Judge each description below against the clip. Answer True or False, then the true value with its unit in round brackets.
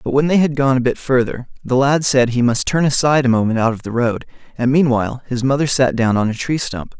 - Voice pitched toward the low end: True (130 Hz)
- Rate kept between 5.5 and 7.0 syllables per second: True (6.0 syllables/s)